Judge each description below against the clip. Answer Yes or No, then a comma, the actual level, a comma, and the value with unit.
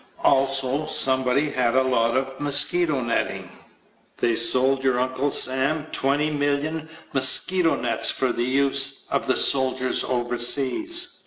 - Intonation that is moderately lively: No, narrow, 2.1 semitones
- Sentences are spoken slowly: Yes, slow, 125 wpm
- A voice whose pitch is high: No, low, 135 Hz